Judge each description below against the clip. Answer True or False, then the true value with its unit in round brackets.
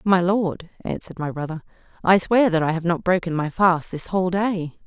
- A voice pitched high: False (175 Hz)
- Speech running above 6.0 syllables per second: False (5.3 syllables/s)